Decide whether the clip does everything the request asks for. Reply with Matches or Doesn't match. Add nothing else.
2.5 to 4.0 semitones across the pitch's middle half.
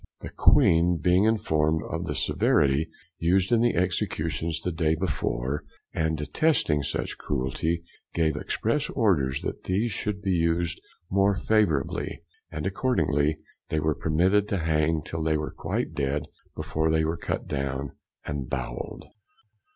Matches